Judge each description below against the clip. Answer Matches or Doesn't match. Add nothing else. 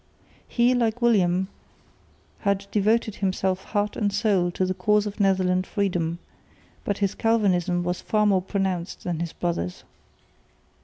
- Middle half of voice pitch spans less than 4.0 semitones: Matches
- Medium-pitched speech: Doesn't match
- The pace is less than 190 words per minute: Matches